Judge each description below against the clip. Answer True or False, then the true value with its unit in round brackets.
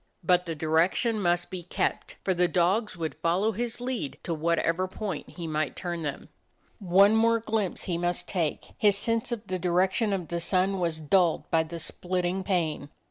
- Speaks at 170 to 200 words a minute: True (185 wpm)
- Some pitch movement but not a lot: True (3.0 semitones)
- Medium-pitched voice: True (180 Hz)